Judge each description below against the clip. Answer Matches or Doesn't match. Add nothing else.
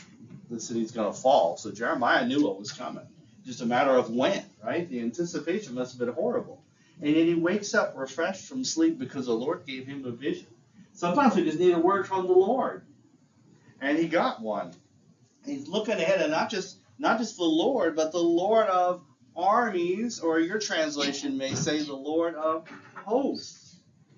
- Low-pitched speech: Doesn't match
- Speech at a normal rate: Matches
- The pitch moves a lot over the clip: Matches